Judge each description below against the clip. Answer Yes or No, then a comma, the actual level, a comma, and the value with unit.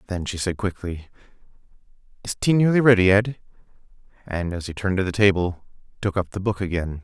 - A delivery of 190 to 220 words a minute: No, average, 180 wpm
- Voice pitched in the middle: No, very low, 95 Hz